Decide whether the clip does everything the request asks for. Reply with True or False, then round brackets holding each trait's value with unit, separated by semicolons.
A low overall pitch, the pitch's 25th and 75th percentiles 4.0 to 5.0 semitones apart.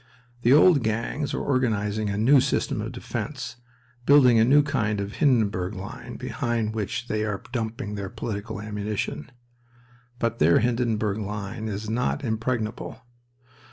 False (110 Hz; 2.7 semitones)